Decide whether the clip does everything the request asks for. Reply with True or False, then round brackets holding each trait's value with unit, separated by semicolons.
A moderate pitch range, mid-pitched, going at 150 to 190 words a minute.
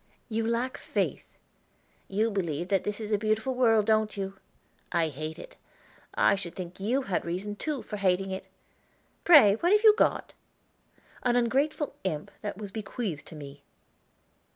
False (3.9 semitones; 210 Hz; 160 wpm)